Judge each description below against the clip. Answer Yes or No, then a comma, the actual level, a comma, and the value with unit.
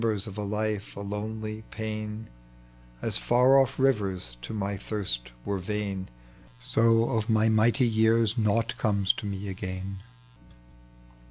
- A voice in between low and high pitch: No, low, 105 Hz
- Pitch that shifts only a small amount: Yes, narrow, 2.1 semitones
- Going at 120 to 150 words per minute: Yes, average, 145 wpm